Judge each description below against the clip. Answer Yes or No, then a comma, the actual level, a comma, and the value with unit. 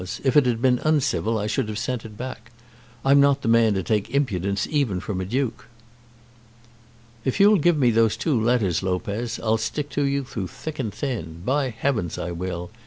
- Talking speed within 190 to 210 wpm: Yes, average, 195 wpm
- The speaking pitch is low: Yes, low, 115 Hz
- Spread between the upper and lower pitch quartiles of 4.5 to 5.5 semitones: Yes, average, 5.1 semitones